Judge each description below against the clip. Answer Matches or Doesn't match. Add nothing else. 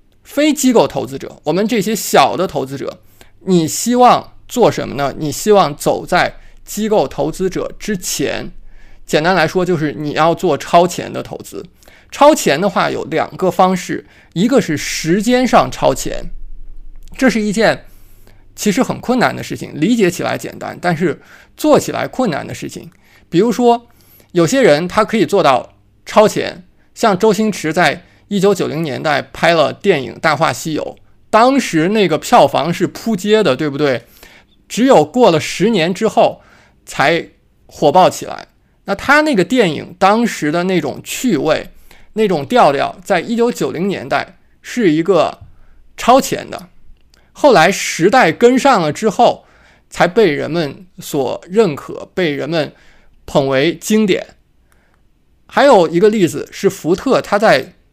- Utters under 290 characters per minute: Matches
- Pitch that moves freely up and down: Matches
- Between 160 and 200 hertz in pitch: Matches